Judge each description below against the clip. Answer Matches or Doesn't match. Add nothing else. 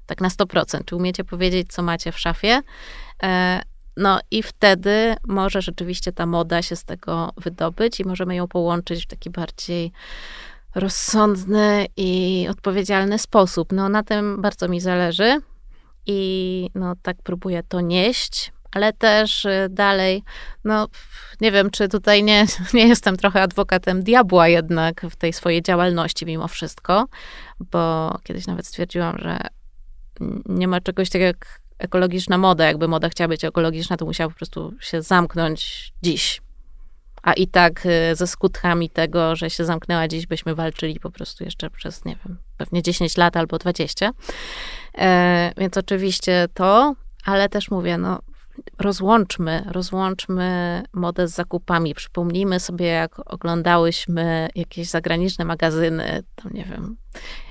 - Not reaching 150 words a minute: Matches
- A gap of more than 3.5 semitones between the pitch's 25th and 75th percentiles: Doesn't match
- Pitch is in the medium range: Matches